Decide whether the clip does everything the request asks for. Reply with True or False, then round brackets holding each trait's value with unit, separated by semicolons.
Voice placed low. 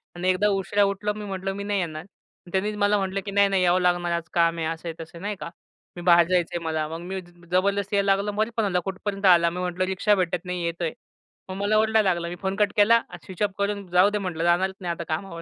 False (185 Hz)